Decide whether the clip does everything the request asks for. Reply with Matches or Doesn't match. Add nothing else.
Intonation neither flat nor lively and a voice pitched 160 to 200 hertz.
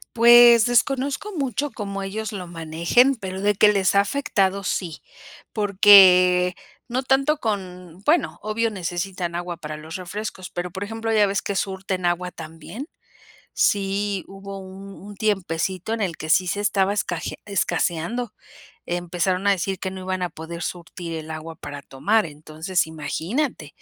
Matches